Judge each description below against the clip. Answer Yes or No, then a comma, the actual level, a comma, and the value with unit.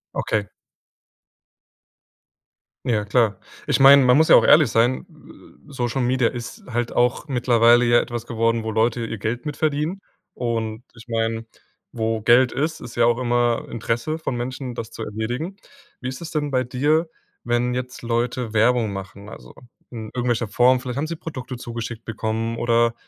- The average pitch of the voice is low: Yes, low, 120 Hz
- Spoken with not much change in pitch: Yes, narrow, 2.1 semitones